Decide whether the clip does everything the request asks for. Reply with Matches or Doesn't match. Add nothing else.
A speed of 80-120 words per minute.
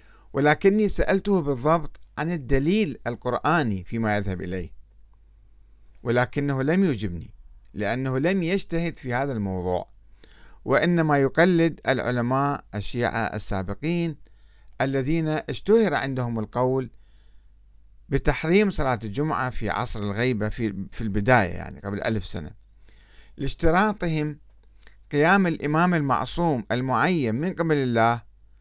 Matches